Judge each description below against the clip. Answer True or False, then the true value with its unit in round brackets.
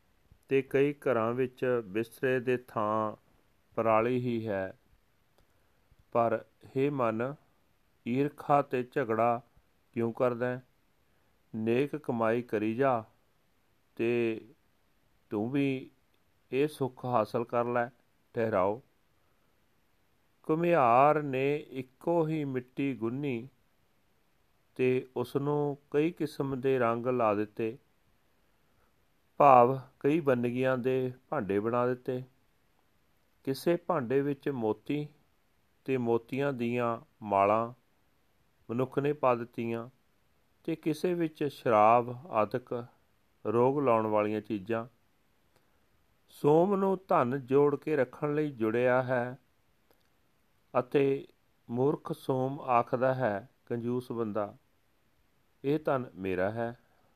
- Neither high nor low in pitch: False (125 Hz)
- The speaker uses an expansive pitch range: False (3.5 semitones)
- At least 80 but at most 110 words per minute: True (100 wpm)